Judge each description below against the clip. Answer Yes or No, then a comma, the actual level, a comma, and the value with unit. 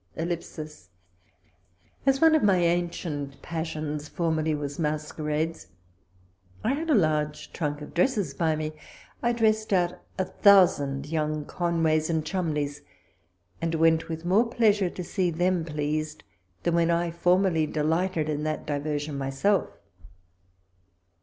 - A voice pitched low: No, medium, 165 Hz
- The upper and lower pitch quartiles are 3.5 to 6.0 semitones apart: No, average, 3.0 semitones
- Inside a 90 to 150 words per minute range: Yes, average, 140 wpm